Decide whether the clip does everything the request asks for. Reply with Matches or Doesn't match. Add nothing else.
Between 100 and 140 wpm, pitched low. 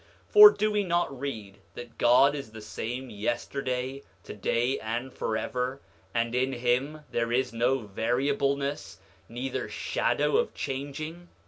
Matches